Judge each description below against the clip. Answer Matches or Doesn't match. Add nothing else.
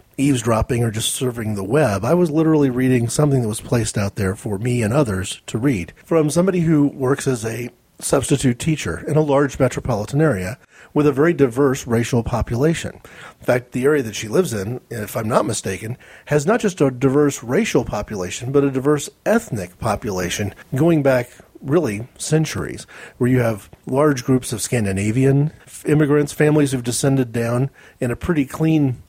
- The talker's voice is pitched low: Matches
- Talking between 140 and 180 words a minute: Matches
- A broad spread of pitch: Doesn't match